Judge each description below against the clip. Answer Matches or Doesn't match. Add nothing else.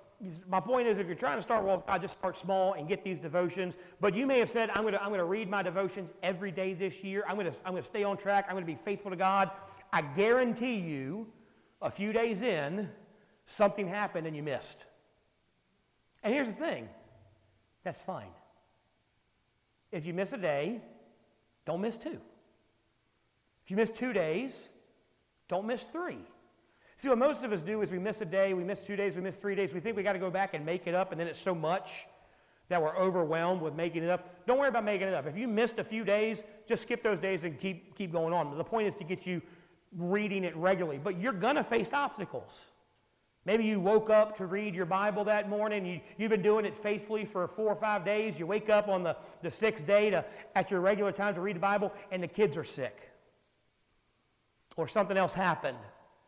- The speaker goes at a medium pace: Doesn't match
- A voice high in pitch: Matches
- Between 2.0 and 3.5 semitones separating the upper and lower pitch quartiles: Matches